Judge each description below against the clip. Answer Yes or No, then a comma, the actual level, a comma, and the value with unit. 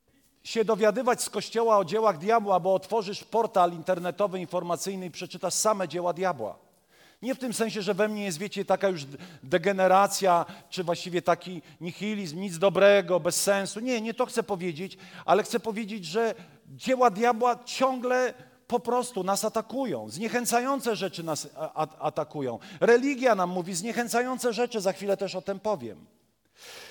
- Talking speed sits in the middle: Yes, average, 150 wpm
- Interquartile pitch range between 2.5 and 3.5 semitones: No, average, 4.1 semitones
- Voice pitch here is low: No, high, 200 Hz